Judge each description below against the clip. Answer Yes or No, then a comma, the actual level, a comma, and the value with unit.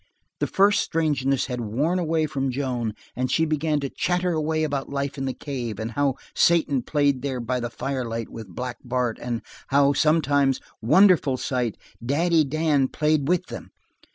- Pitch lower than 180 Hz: Yes, medium, 140 Hz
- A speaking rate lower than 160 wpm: No, average, 170 wpm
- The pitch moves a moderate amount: Yes, average, 3.7 semitones